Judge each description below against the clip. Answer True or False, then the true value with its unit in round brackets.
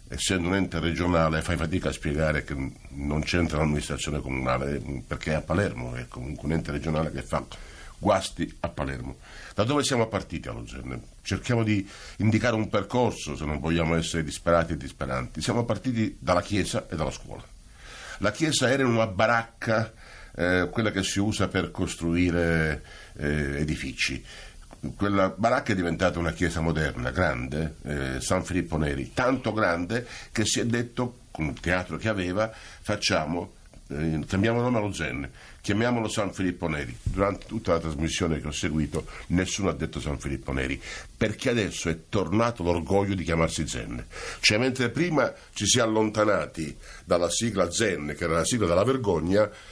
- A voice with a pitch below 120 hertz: True (85 Hz)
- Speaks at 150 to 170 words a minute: True (165 wpm)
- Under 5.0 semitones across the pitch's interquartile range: False (5.6 semitones)